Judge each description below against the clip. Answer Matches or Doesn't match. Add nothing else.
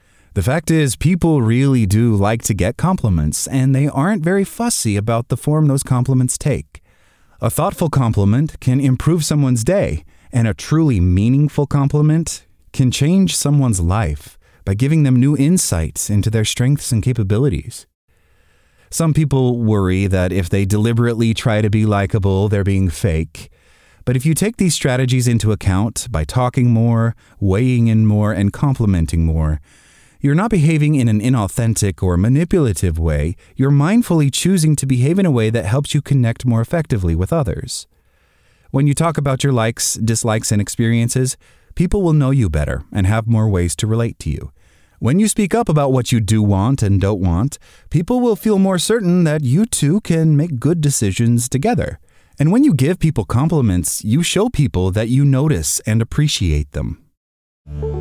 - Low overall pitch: Matches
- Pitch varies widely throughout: Matches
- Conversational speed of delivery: Matches